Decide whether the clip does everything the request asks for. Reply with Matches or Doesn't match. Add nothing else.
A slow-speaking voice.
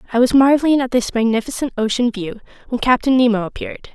Doesn't match